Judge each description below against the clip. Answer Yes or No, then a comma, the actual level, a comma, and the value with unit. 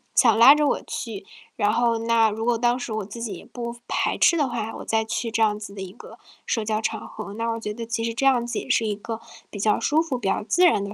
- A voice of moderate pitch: No, high, 230 Hz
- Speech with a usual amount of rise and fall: No, narrow, 2.1 semitones